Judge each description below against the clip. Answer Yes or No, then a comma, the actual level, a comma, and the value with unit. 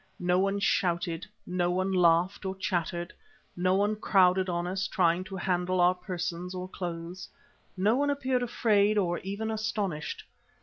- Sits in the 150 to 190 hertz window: Yes, medium, 185 Hz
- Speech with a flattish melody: Yes, narrow, 2.3 semitones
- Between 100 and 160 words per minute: Yes, average, 155 wpm